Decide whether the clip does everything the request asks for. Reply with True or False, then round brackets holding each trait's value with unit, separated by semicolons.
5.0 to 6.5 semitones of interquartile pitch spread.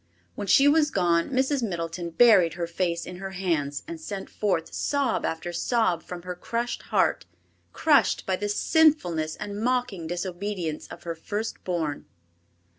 True (5.6 semitones)